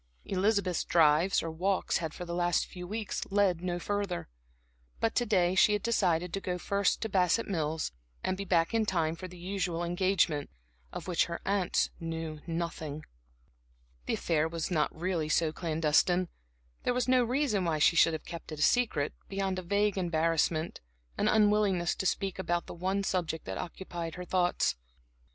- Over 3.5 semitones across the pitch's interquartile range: No, average, 3.0 semitones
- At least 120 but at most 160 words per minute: No, average, 175 wpm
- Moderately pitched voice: Yes, medium, 180 Hz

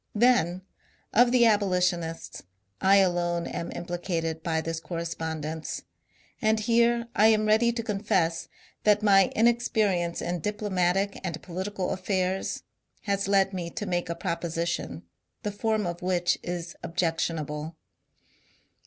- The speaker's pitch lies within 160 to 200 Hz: Yes, medium, 185 Hz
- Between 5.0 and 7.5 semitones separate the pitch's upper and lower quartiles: No, average, 3.7 semitones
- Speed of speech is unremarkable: No, slow, 125 wpm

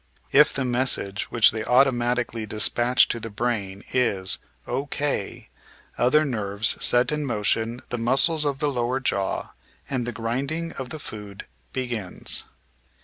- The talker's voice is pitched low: Yes, low, 120 Hz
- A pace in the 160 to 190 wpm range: No, average, 140 wpm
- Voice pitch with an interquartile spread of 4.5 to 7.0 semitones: No, average, 3.5 semitones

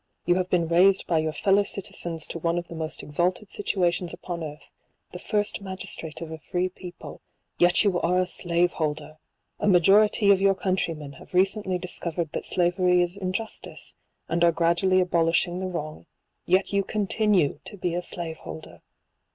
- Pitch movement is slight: Yes, narrow, 2.2 semitones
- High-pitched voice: No, medium, 175 Hz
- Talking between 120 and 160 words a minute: No, average, 175 wpm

